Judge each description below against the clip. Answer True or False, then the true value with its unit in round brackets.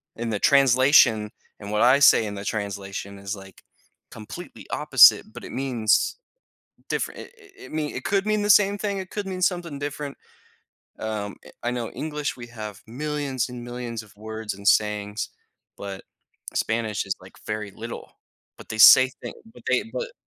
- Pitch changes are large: True (5.8 semitones)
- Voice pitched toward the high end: False (120 Hz)